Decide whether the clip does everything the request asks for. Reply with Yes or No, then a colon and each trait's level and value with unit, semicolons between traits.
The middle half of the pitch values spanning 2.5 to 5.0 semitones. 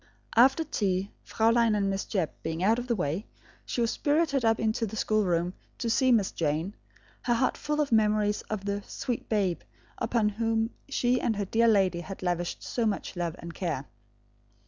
Yes: average, 3.9 semitones